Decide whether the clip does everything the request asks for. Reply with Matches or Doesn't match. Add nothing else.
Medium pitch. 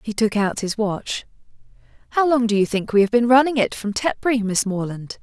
Doesn't match